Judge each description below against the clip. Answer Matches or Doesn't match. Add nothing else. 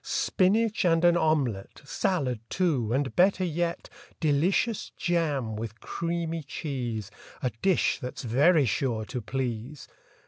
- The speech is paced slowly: Matches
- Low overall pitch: Doesn't match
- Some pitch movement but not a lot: Doesn't match